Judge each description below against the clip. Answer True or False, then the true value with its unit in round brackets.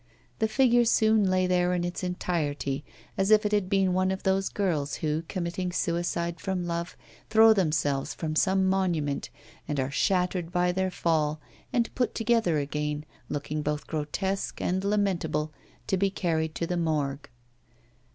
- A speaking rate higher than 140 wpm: True (160 wpm)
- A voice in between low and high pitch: True (180 Hz)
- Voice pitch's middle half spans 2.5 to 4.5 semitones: True (3.9 semitones)